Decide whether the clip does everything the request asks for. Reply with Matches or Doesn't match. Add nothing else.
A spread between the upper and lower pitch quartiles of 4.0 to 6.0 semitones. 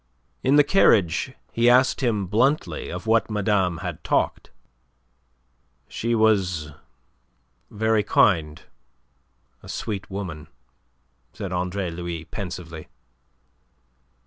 Matches